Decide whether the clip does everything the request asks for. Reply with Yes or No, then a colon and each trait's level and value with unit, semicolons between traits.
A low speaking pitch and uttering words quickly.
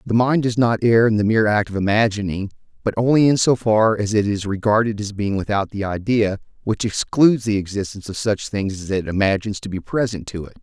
Yes: low, 105 Hz; fast, 225 wpm